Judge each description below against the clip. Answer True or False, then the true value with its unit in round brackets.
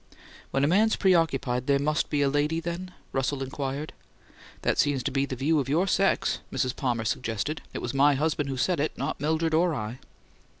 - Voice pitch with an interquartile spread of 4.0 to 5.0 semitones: False (3.2 semitones)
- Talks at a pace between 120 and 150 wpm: False (200 wpm)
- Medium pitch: True (145 Hz)